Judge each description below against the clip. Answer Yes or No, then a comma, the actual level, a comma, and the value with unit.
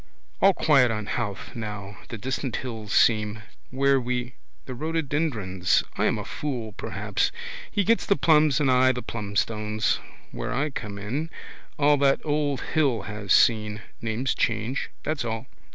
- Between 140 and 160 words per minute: Yes, average, 150 wpm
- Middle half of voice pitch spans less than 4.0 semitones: No, average, 4.9 semitones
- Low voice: Yes, low, 125 Hz